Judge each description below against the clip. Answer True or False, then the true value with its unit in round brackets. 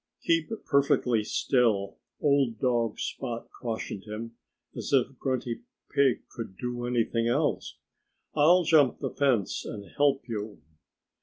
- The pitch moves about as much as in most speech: True (3.5 semitones)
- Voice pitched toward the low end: True (120 Hz)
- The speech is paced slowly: True (125 wpm)